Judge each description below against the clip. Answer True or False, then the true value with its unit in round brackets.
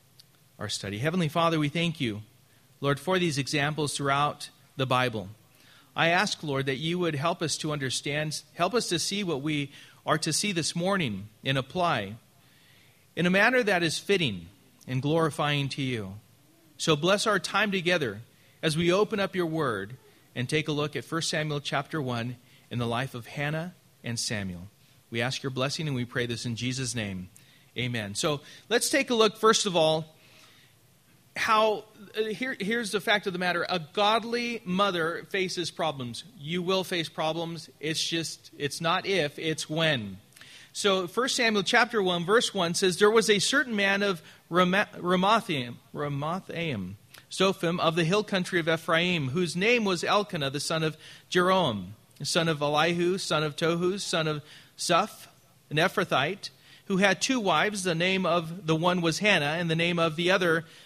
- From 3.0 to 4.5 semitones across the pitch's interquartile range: False (5.1 semitones)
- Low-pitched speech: False (160 Hz)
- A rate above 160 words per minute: True (175 wpm)